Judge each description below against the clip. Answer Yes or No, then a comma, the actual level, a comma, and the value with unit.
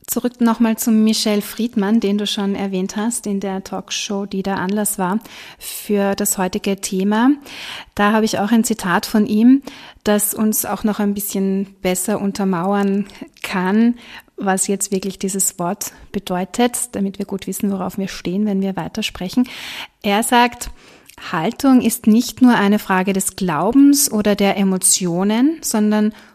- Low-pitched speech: No, high, 205 Hz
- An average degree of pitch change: No, narrow, 2.3 semitones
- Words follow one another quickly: No, average, 155 wpm